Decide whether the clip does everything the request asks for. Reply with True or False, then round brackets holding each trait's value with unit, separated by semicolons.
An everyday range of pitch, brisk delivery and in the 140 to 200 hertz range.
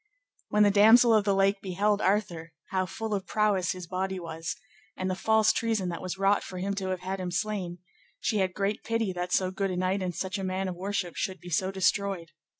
False (1.9 semitones; 230 wpm; 190 Hz)